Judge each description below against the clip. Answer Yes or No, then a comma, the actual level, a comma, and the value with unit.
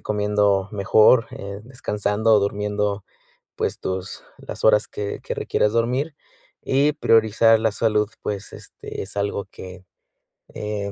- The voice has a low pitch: Yes, low, 105 Hz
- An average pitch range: No, narrow, 1.8 semitones